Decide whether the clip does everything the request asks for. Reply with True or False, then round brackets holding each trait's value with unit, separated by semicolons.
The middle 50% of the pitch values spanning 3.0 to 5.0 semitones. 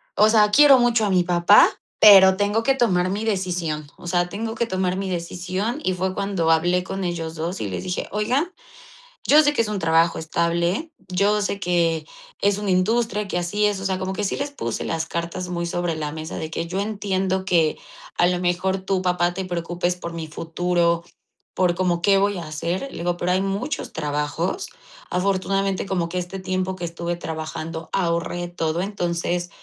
False (2.5 semitones)